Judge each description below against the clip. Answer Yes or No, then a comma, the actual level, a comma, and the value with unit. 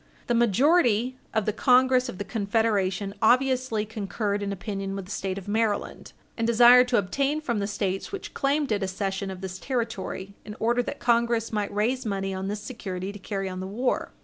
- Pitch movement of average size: Yes, average, 3.7 semitones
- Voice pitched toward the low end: No, high, 215 Hz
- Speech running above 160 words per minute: Yes, average, 200 wpm